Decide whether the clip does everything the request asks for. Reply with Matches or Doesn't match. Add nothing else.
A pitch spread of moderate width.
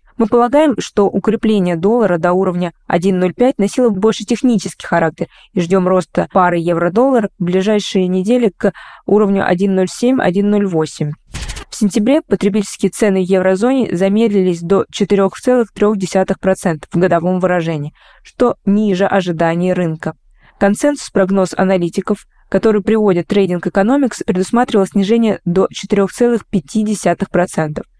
Matches